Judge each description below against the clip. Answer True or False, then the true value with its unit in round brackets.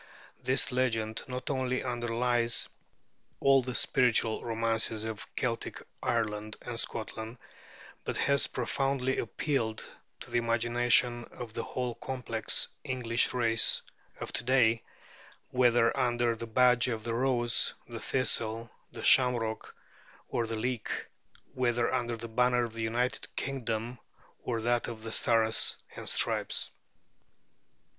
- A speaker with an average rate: False (125 wpm)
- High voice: False (120 Hz)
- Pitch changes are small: True (1.8 semitones)